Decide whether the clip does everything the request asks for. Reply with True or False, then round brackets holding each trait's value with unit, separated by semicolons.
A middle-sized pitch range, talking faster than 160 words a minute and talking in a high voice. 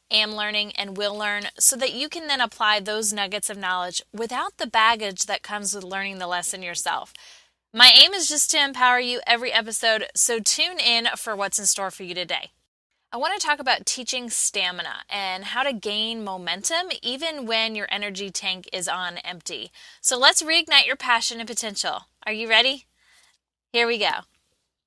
True (4.0 semitones; 185 wpm; 220 Hz)